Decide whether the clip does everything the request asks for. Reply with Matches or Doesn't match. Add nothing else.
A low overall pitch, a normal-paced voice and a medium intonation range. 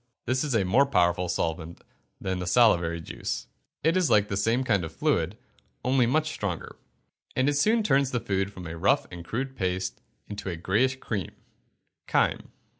Doesn't match